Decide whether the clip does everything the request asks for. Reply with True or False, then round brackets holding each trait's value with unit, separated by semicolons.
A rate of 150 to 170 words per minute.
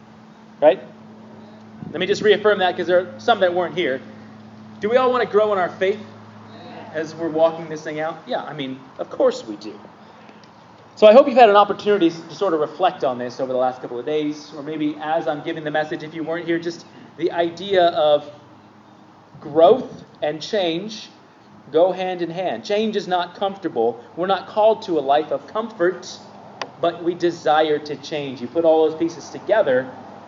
False (195 wpm)